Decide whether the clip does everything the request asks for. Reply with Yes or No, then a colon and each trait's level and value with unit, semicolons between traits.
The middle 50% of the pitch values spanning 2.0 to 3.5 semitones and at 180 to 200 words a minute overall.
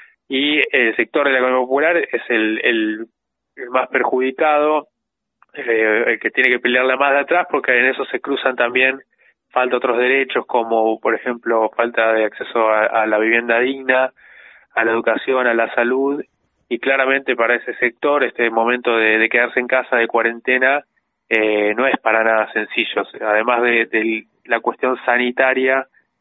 No: narrow, 2.5 semitones; average, 170 wpm